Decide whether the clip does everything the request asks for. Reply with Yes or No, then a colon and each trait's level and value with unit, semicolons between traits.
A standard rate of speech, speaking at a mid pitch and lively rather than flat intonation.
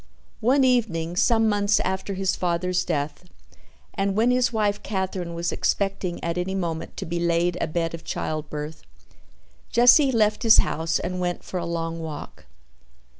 No: average, 155 wpm; medium, 180 Hz; average, 4.0 semitones